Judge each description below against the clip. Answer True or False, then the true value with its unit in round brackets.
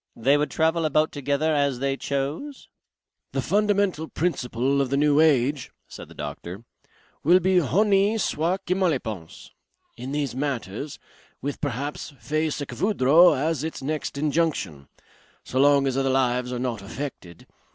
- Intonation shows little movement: False (3.6 semitones)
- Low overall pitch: False (145 Hz)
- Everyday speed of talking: True (160 wpm)